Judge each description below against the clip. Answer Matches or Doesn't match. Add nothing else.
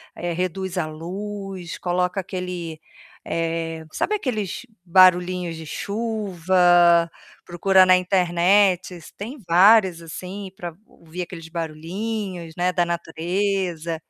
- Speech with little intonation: Matches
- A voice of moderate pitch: Matches